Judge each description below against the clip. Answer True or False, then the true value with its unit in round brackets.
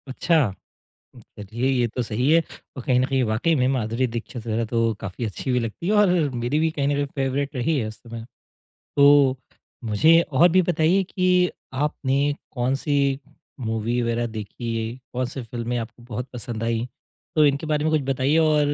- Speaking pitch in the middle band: False (130 Hz)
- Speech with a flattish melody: False (4.0 semitones)